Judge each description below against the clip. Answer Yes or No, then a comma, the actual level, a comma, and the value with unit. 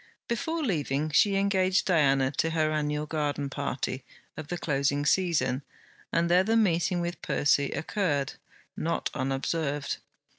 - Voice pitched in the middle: Yes, medium, 155 Hz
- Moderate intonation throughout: Yes, average, 4.2 semitones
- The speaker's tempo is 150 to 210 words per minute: No, slow, 135 wpm